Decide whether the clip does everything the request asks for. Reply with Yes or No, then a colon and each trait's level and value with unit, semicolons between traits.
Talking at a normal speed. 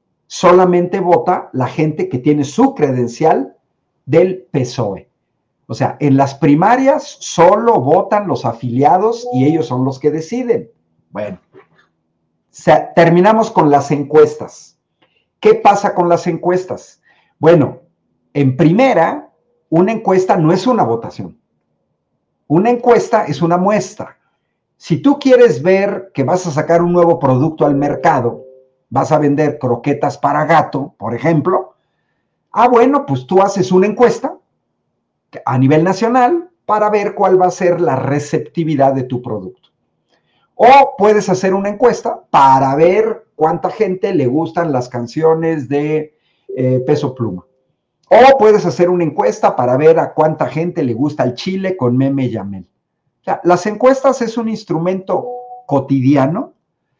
Yes: average, 140 wpm